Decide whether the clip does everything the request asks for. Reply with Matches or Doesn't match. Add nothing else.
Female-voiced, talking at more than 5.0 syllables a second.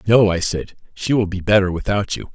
Doesn't match